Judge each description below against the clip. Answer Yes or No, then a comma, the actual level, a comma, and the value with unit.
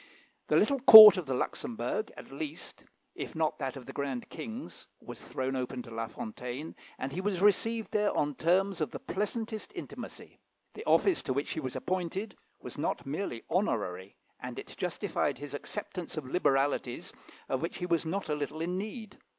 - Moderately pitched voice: Yes, medium, 165 Hz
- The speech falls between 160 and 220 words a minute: Yes, average, 185 wpm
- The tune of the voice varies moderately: No, wide, 7.5 semitones